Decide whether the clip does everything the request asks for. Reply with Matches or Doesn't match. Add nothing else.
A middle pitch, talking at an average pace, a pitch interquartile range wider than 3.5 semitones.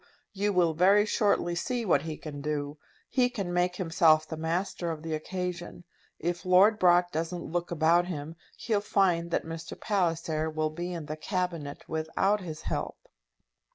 Doesn't match